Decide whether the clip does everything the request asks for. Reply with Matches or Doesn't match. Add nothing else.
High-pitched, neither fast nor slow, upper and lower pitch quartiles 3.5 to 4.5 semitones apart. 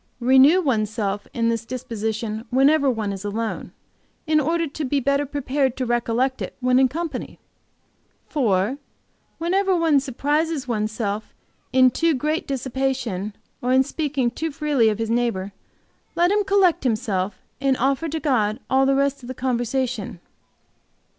Matches